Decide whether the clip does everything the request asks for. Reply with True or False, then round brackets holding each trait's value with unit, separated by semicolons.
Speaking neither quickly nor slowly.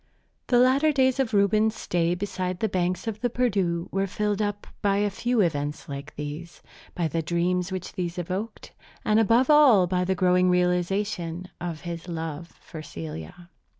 True (170 wpm)